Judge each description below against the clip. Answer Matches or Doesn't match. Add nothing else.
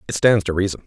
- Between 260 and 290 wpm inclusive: Matches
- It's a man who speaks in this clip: Matches